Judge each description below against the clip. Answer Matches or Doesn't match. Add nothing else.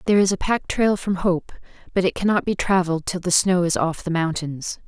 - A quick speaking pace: Matches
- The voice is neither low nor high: Matches